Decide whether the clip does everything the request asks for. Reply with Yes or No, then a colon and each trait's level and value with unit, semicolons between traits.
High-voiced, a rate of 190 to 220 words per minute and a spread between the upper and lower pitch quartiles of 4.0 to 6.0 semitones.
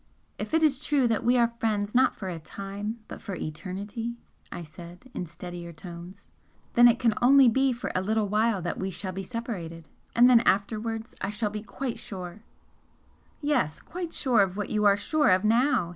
Yes: high, 210 Hz; average, 200 wpm; average, 4.4 semitones